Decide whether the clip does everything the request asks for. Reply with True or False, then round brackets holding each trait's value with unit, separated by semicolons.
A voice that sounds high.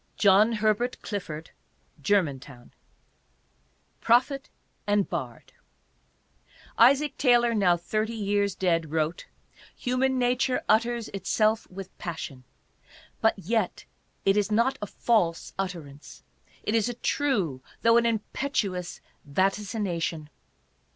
True (205 Hz)